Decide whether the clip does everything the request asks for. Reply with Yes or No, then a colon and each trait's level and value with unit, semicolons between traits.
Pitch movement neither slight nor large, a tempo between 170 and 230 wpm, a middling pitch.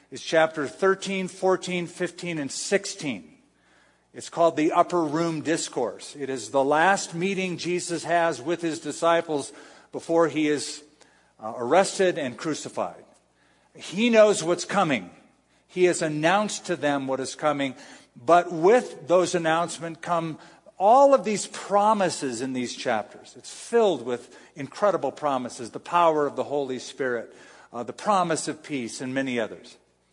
No: average, 4.1 semitones; average, 145 wpm; medium, 165 Hz